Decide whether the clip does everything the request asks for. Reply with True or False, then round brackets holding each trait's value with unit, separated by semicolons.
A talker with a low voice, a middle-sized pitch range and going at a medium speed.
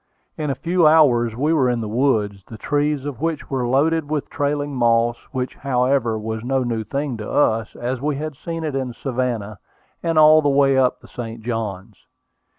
True (130 Hz; 4.0 semitones; 195 wpm)